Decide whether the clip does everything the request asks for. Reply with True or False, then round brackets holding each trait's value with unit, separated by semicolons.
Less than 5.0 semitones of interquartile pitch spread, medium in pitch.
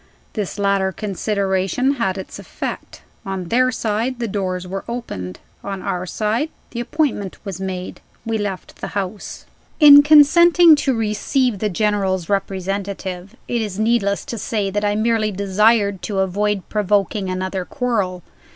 False (3.3 semitones; 205 Hz)